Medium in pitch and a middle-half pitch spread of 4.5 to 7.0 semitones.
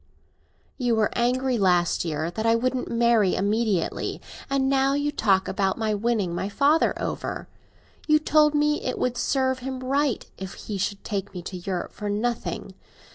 No: high, 230 Hz; average, 5.1 semitones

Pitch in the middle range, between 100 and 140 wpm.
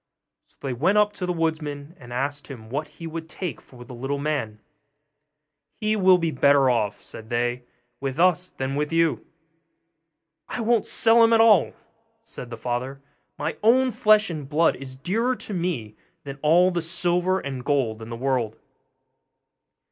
No: medium, 150 Hz; average, 170 wpm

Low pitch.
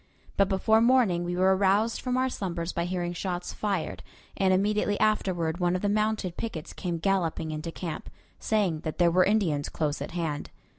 No: medium, 185 Hz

